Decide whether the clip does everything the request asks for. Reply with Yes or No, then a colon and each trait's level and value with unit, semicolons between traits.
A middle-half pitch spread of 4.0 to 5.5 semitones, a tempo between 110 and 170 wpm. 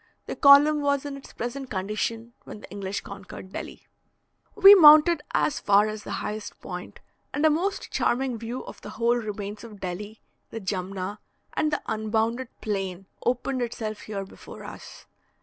Yes: average, 5.2 semitones; average, 165 wpm